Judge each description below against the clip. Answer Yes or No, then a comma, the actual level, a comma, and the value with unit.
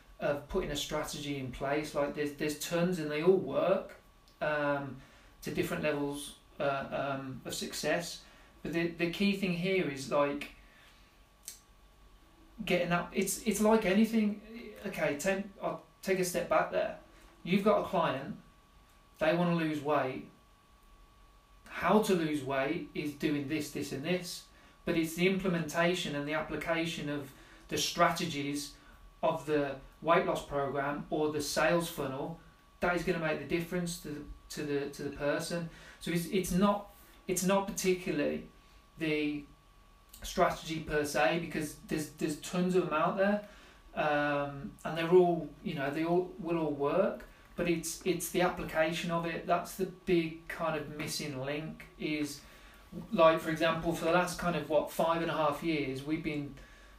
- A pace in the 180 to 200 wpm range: No, average, 165 wpm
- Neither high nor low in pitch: Yes, medium, 160 Hz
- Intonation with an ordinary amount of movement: Yes, average, 3.3 semitones